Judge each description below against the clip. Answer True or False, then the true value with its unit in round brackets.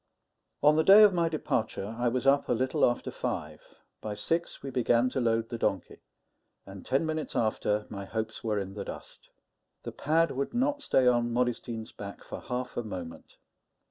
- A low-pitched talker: True (120 Hz)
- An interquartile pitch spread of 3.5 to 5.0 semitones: True (4.6 semitones)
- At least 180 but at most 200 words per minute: True (185 wpm)